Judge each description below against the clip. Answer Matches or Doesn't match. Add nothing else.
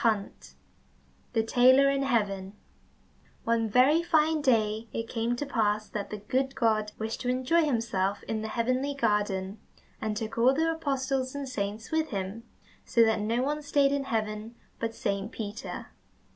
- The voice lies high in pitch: Matches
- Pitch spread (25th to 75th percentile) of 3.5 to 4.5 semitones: Matches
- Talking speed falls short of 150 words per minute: Doesn't match